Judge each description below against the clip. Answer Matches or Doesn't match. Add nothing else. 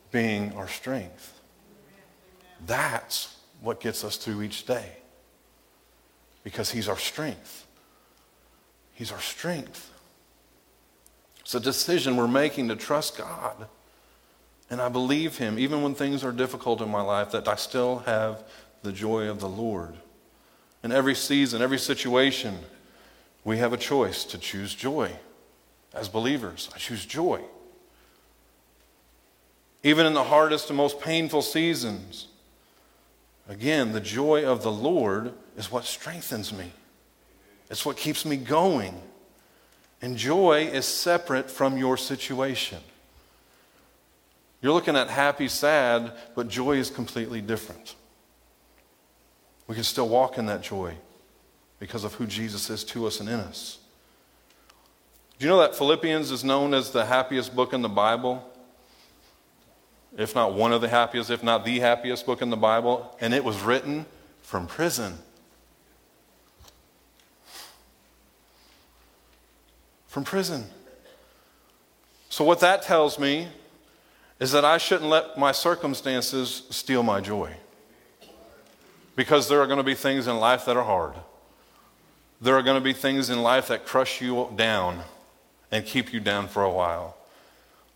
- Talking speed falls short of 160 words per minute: Matches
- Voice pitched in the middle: Doesn't match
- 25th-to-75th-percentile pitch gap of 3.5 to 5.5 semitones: Matches